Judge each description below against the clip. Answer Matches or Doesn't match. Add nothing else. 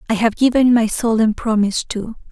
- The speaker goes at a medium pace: Matches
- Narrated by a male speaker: Doesn't match